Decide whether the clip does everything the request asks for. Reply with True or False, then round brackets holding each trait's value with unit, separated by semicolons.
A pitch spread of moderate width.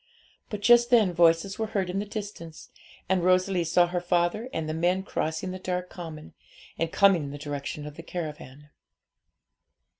True (3.3 semitones)